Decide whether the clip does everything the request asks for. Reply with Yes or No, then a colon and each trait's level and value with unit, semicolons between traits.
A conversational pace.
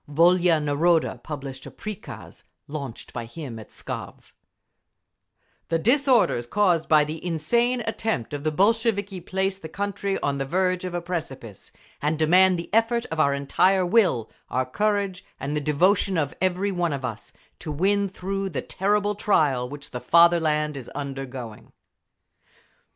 Yes: average, 150 wpm